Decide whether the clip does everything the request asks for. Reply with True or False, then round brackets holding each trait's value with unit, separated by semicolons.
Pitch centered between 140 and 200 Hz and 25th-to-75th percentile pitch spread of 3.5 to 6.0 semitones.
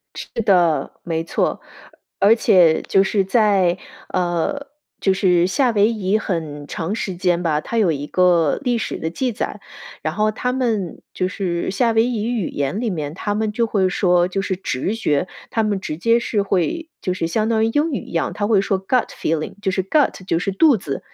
True (195 Hz; 4.2 semitones)